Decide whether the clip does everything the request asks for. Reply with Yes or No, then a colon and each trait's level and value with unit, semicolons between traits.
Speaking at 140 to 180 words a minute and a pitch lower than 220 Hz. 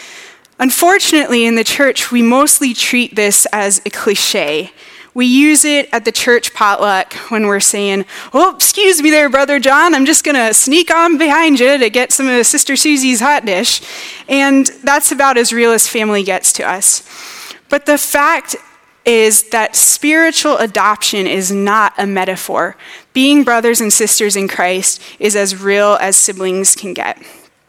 No: average, 165 wpm; high, 245 Hz